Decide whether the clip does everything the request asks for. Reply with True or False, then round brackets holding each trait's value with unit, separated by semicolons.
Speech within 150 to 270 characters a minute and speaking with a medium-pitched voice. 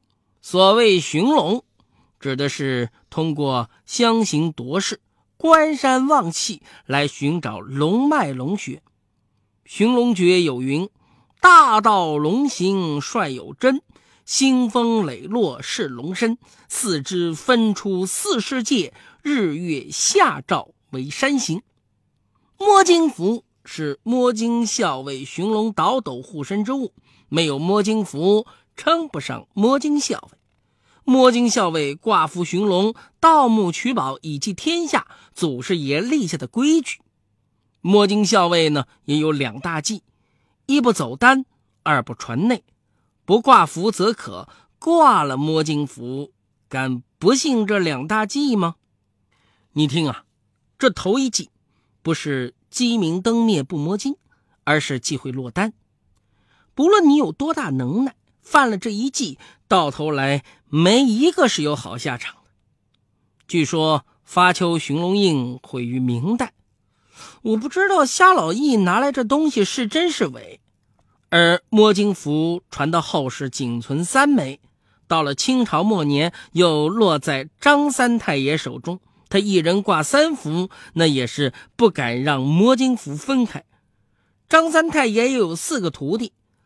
True (190 characters per minute; 180 Hz)